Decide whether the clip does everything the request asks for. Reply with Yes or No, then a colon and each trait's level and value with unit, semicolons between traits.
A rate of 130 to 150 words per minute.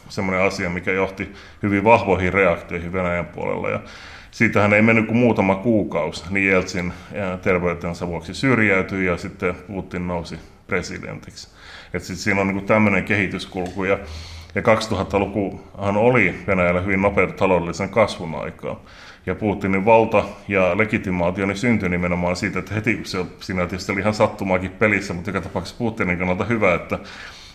Yes: average, 140 wpm